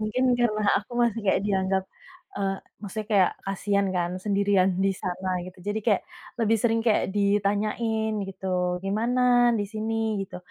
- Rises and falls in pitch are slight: Yes, narrow, 2.1 semitones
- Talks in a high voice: Yes, high, 205 Hz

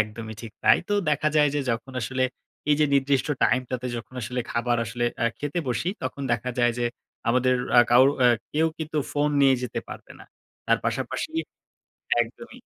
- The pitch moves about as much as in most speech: Yes, average, 3.2 semitones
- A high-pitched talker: No, low, 130 Hz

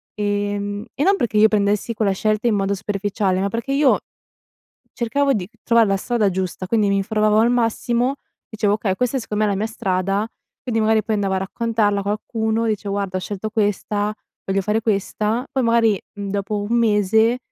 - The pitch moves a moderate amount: No, narrow, 2.2 semitones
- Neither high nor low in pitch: No, high, 210 Hz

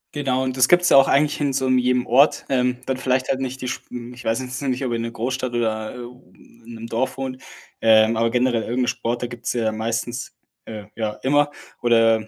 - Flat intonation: Yes, narrow, 2.2 semitones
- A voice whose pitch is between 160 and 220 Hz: No, low, 125 Hz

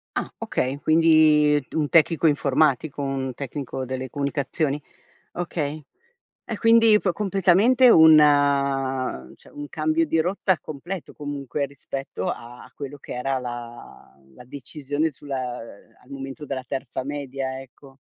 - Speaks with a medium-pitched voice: Yes, medium, 145 Hz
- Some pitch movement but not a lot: Yes, average, 3.1 semitones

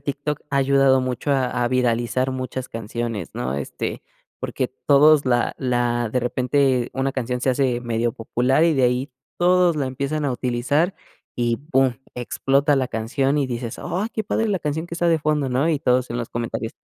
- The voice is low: Yes, low, 130 Hz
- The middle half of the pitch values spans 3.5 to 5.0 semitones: No, average, 2.9 semitones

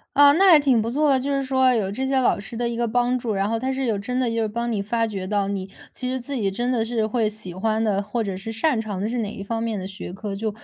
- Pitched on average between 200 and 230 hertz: Yes, high, 225 Hz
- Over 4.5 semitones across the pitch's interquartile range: No, average, 3.6 semitones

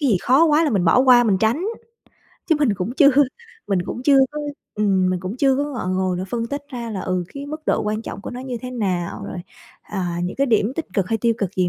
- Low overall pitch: No, high, 230 Hz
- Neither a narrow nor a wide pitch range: No, wide, 6.3 semitones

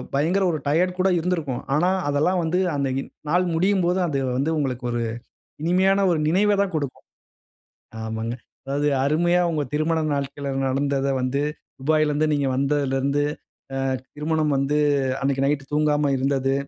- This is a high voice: No, medium, 150 Hz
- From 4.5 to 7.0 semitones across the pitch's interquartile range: No, average, 3.5 semitones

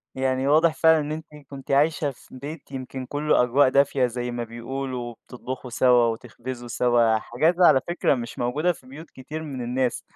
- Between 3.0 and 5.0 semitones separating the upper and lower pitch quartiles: Yes, average, 3.3 semitones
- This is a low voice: Yes, low, 130 Hz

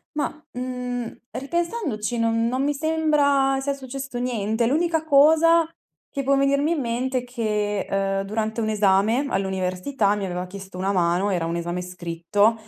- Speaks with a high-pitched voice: Yes, high, 235 Hz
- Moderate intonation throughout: No, wide, 6.0 semitones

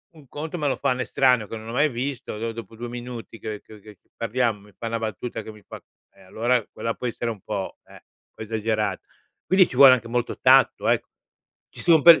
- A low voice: Yes, low, 115 Hz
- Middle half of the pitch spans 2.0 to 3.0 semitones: Yes, average, 2.7 semitones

